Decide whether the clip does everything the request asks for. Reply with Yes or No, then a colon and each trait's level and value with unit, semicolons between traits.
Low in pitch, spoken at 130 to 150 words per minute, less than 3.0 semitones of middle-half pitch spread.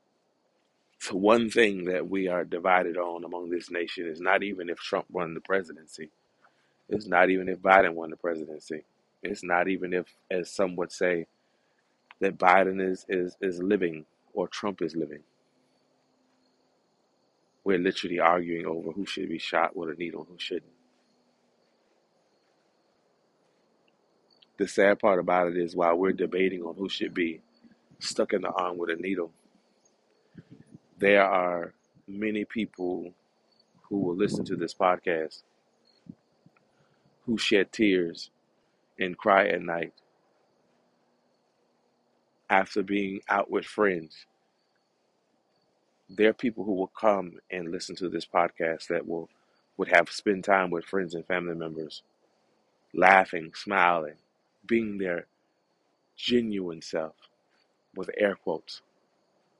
Yes: very low, 90 Hz; slow, 135 wpm; narrow, 2.4 semitones